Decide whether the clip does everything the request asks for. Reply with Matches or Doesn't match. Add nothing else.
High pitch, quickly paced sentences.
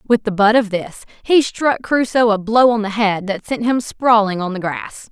Matches